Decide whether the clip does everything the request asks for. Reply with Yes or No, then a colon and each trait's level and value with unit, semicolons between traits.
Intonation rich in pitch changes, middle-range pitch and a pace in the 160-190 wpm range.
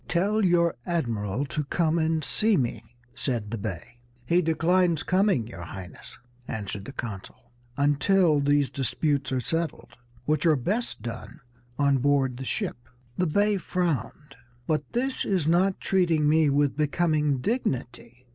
No: wide, 5.8 semitones; medium, 150 Hz; average, 145 wpm